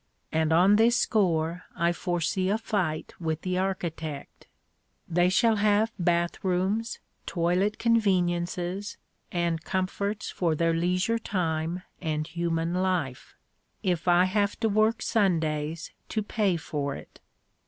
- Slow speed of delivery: Yes, slow, 125 wpm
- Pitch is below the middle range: No, medium, 180 Hz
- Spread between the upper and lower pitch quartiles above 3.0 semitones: Yes, average, 3.5 semitones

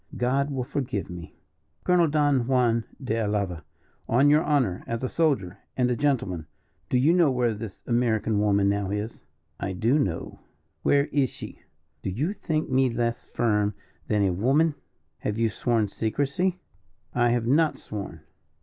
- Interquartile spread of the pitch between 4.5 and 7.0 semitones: Yes, average, 5.0 semitones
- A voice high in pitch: No, low, 120 Hz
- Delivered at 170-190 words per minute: No, average, 160 wpm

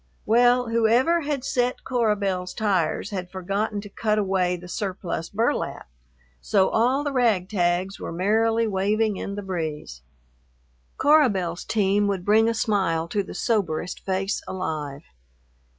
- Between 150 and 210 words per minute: No, average, 140 wpm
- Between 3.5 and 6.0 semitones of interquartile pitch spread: Yes, average, 3.8 semitones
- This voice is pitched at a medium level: No, high, 200 Hz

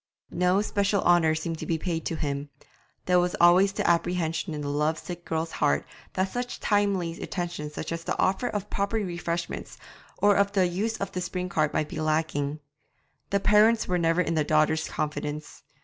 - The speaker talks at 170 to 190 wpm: Yes, average, 180 wpm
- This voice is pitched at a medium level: Yes, medium, 175 Hz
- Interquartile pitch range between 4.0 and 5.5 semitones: No, average, 3.6 semitones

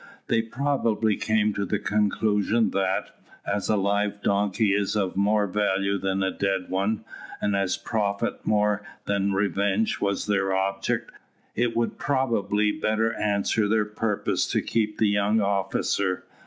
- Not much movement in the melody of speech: Yes, narrow, 1.6 semitones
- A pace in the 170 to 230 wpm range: No, average, 145 wpm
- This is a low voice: Yes, low, 105 Hz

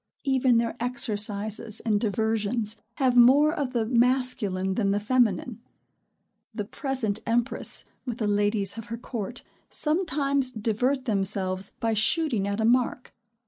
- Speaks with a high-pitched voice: Yes, high, 230 Hz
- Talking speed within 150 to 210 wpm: No, slow, 135 wpm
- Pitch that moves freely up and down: No, average, 3.6 semitones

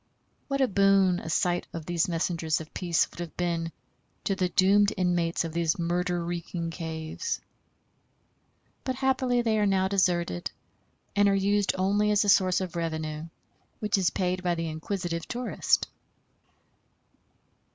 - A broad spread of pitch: No, average, 3.1 semitones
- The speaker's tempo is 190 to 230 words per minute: No, average, 150 wpm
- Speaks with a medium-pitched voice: Yes, medium, 180 Hz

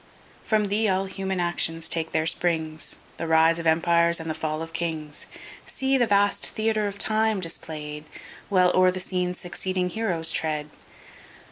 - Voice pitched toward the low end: No, medium, 175 Hz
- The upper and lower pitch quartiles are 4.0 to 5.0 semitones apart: No, average, 3.4 semitones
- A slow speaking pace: No, average, 160 wpm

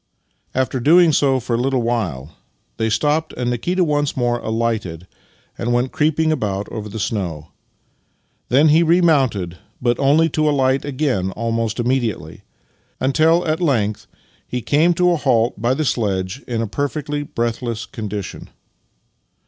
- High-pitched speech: No, low, 125 Hz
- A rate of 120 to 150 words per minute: Yes, average, 145 wpm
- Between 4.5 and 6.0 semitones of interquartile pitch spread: Yes, average, 4.8 semitones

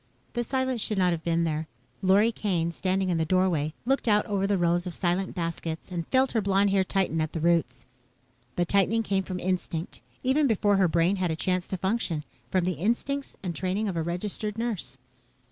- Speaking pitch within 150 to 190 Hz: Yes, medium, 185 Hz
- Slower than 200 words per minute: No, fast, 205 wpm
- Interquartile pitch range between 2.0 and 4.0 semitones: Yes, average, 3.4 semitones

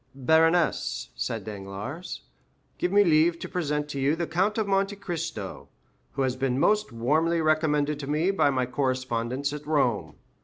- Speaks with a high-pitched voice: No, medium, 150 Hz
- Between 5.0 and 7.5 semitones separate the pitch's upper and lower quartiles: No, average, 4.6 semitones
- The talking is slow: No, average, 160 wpm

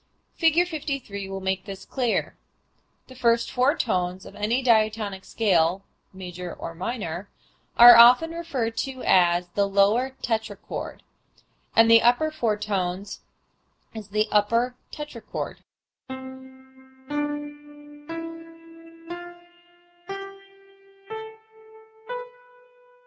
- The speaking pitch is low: No, high, 220 Hz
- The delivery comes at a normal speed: No, slow, 90 wpm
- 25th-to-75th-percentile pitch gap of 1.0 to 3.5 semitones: No, average, 4.4 semitones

